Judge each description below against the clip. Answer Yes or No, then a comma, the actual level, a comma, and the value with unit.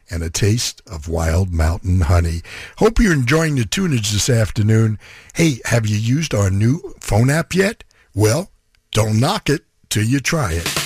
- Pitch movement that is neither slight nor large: No, wide, 7.1 semitones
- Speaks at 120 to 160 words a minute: No, average, 170 wpm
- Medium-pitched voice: No, low, 110 Hz